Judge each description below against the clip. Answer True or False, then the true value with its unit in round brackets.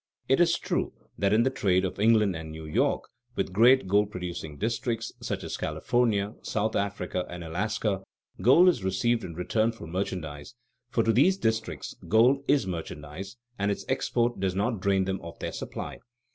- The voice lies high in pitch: False (100 Hz)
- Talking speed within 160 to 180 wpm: True (175 wpm)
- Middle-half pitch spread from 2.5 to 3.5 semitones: False (4.1 semitones)